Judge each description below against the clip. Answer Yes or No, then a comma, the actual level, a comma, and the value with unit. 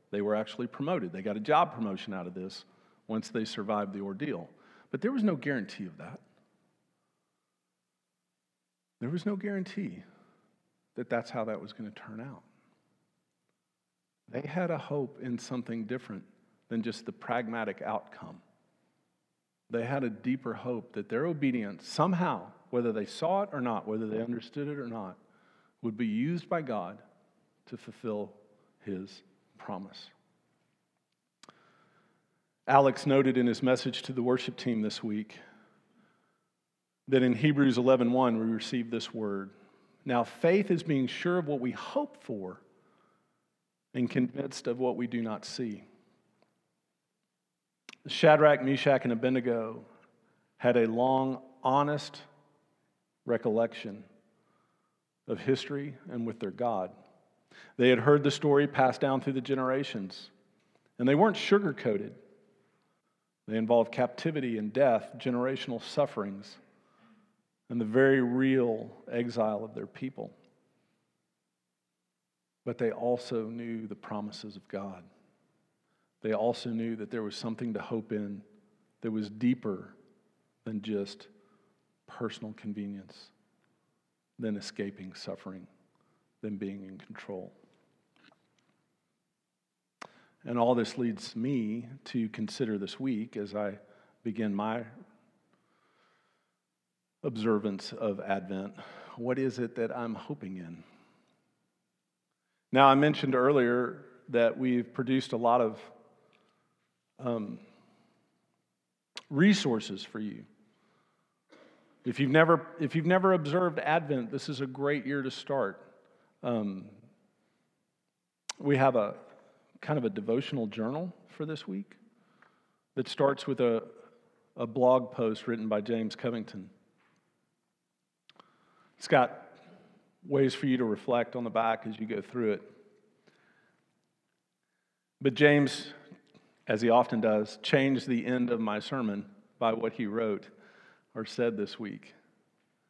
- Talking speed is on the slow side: Yes, slow, 125 wpm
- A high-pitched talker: No, low, 125 Hz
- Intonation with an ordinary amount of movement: Yes, average, 4.4 semitones